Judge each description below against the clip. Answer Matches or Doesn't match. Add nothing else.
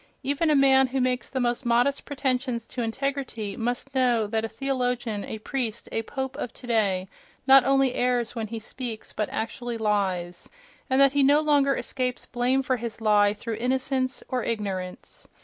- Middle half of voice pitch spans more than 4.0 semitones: Doesn't match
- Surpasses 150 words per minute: Matches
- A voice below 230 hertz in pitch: Doesn't match